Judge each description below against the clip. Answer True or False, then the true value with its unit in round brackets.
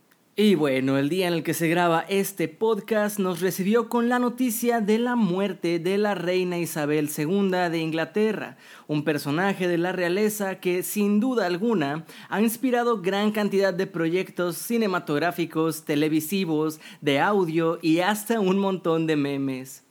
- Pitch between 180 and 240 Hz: True (185 Hz)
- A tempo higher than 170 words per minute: False (155 wpm)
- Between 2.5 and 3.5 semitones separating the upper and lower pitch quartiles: False (4.3 semitones)